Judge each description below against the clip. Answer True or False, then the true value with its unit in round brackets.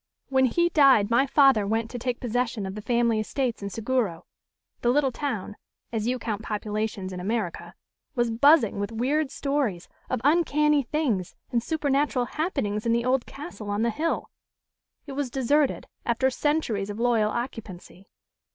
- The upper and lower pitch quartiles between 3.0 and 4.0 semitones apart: False (4.5 semitones)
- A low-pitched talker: False (240 Hz)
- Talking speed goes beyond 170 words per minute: False (160 wpm)